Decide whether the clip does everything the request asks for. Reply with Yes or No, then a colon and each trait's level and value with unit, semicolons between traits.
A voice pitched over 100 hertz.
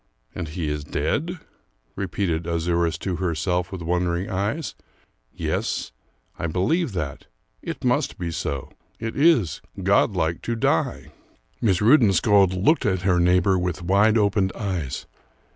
No: very low, 90 Hz